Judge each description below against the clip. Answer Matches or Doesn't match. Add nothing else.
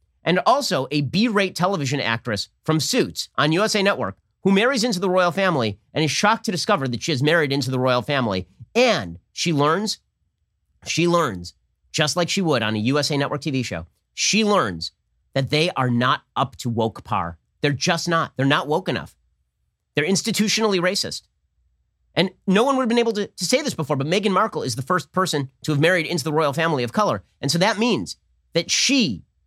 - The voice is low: Doesn't match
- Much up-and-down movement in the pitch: Matches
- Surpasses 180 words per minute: Matches